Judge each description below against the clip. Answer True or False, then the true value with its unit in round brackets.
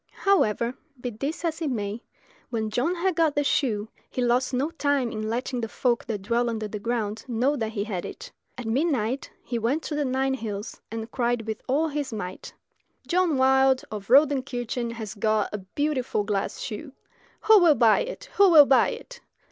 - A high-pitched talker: True (245 Hz)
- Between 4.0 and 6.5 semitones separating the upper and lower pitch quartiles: True (4.7 semitones)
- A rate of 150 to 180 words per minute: False (190 wpm)